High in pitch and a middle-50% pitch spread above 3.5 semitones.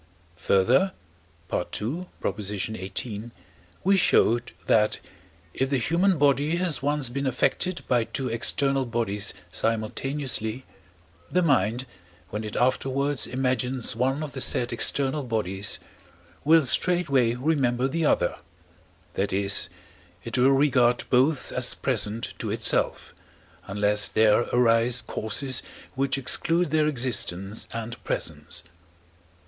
No: low, 125 Hz; average, 4.0 semitones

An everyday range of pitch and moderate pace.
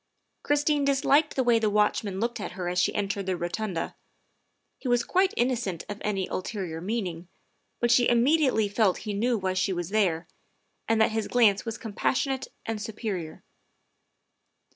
Yes: average, 4.2 semitones; average, 165 wpm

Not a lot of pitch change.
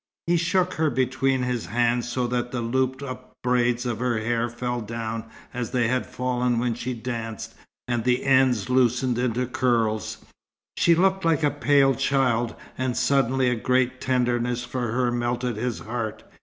Yes: narrow, 1.4 semitones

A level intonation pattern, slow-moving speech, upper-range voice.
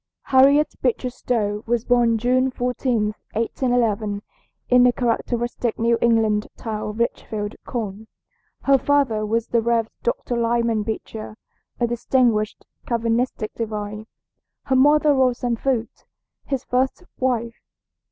Yes: narrow, 2.3 semitones; slow, 120 wpm; high, 235 Hz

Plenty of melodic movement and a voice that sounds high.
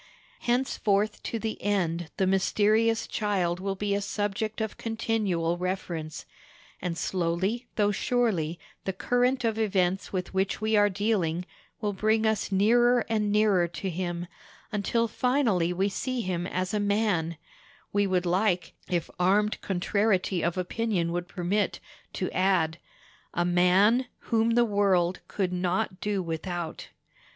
No: average, 3.5 semitones; high, 195 Hz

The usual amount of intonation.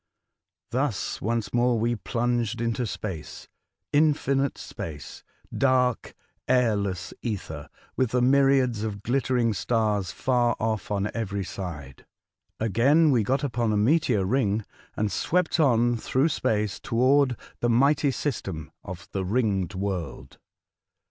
Yes: average, 4.2 semitones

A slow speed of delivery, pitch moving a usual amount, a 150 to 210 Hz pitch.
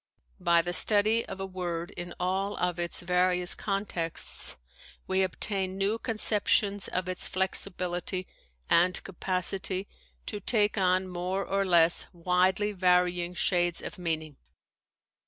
No: slow, 125 wpm; narrow, 1.9 semitones; medium, 185 Hz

